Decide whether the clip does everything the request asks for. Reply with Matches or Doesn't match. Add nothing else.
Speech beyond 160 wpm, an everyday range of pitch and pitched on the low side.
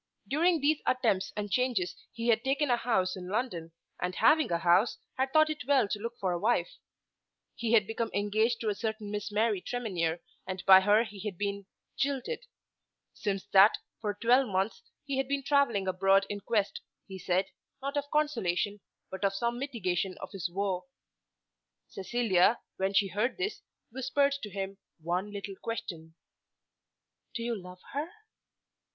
Doesn't match